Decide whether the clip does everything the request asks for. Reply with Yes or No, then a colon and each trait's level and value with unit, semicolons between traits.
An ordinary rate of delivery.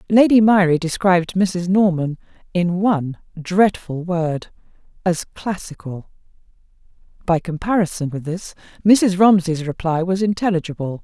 No: slow, 110 wpm